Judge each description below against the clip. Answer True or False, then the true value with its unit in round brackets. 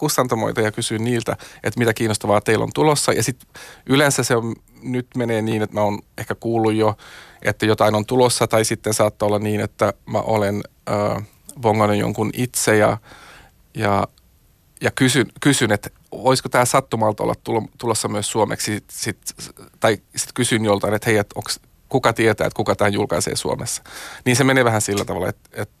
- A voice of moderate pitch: False (110 Hz)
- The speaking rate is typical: False (180 wpm)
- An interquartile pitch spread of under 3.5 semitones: True (2.7 semitones)